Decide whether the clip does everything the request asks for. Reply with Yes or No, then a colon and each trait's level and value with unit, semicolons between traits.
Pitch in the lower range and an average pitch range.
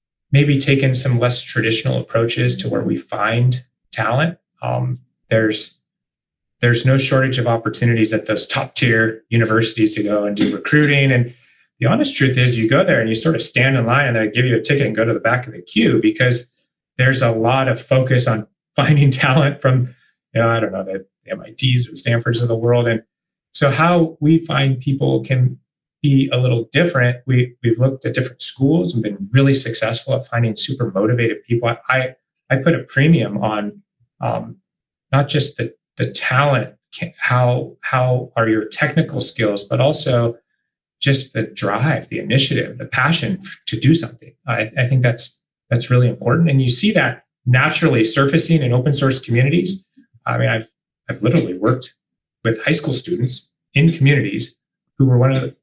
Yes: low, 125 Hz; average, 3.4 semitones